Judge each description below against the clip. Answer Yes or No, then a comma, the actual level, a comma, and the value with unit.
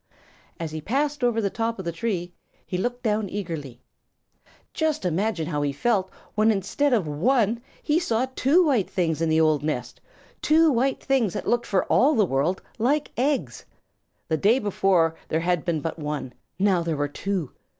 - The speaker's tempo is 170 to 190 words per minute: Yes, average, 180 wpm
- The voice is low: No, high, 195 Hz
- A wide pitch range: Yes, wide, 6.9 semitones